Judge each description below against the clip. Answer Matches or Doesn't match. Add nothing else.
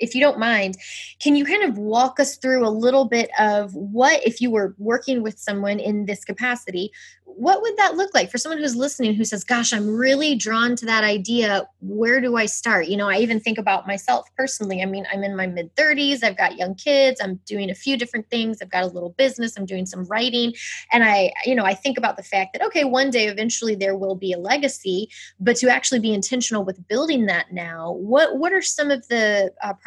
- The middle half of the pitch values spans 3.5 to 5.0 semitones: Matches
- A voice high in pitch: Matches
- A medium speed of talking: Doesn't match